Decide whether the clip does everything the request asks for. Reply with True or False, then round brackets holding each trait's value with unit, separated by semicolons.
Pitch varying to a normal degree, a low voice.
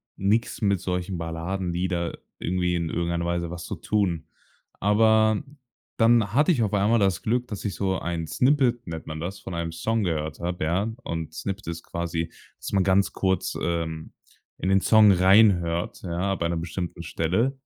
True (3.5 semitones; 90 Hz)